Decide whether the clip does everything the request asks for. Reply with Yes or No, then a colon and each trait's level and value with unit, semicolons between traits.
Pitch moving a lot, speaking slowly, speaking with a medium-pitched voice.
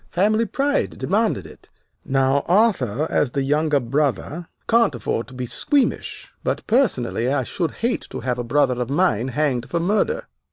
No: wide, 8.2 semitones; average, 165 wpm; medium, 145 Hz